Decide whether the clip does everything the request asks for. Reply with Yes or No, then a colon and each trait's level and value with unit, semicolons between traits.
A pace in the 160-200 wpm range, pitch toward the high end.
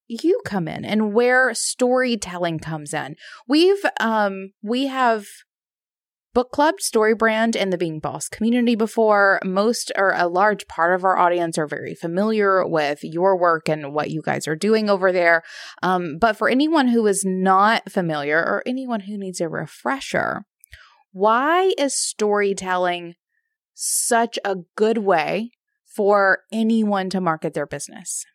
No: average, 150 wpm; high, 205 Hz